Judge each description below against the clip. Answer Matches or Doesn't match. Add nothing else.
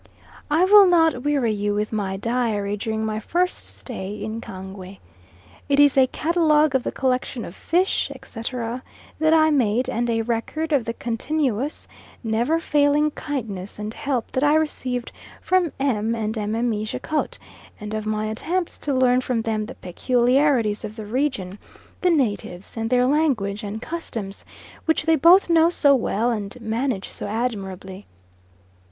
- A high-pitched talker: Matches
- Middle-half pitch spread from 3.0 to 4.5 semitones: Doesn't match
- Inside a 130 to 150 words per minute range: Doesn't match